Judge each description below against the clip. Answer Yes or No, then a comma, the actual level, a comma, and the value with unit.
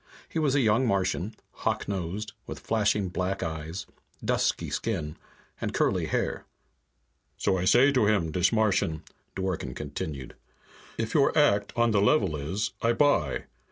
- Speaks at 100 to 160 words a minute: Yes, average, 150 wpm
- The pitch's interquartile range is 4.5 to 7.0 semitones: Yes, average, 4.9 semitones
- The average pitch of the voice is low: Yes, low, 100 Hz